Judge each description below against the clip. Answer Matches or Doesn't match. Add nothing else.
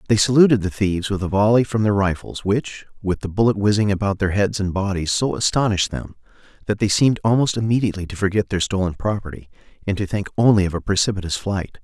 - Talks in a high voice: Doesn't match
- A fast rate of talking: Matches